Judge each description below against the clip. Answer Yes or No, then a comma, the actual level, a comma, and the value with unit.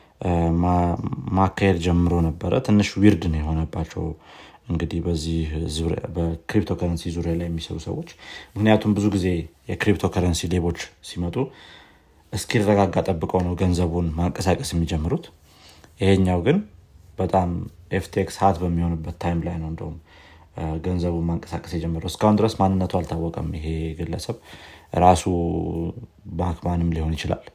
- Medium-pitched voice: No, very low, 85 Hz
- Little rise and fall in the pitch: Yes, narrow, 2.1 semitones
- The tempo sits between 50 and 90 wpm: No, average, 105 wpm